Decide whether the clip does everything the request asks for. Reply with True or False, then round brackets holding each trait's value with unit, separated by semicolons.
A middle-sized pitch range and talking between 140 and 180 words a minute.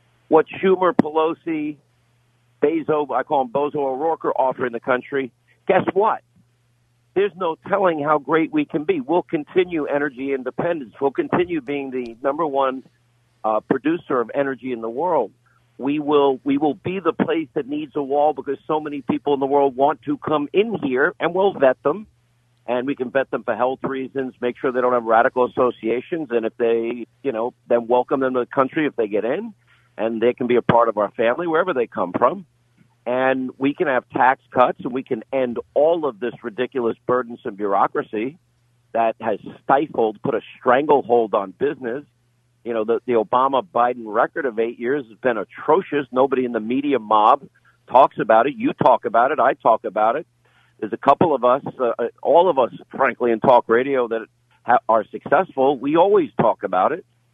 False (4.0 semitones; 195 wpm)